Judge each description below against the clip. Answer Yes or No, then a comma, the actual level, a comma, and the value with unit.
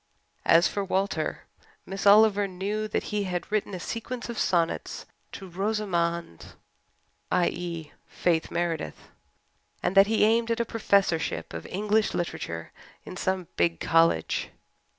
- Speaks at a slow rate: Yes, slow, 130 wpm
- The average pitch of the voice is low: No, high, 195 Hz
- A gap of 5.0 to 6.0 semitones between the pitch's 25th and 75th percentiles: No, average, 3.7 semitones